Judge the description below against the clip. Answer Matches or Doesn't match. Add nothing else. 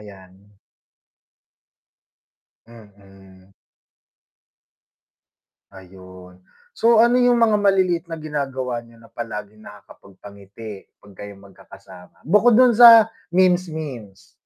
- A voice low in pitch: Matches